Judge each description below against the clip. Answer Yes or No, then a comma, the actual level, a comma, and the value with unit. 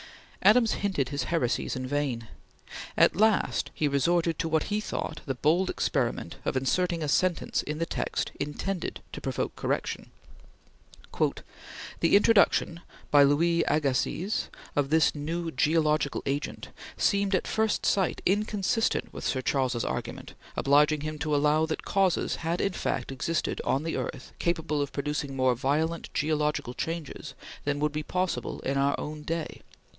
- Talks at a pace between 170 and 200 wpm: No, average, 150 wpm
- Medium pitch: Yes, medium, 155 Hz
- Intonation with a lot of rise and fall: No, average, 3.4 semitones